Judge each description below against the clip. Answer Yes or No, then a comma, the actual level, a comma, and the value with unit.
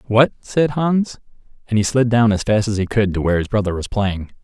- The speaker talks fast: Yes, fast, 245 wpm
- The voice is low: Yes, low, 110 Hz